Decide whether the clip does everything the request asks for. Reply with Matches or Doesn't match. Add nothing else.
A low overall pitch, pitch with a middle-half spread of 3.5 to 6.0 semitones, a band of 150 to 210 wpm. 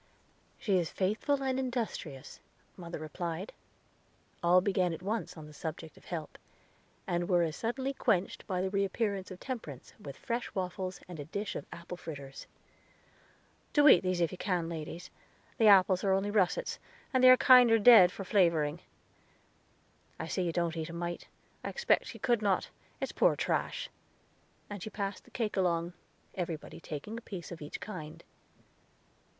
Doesn't match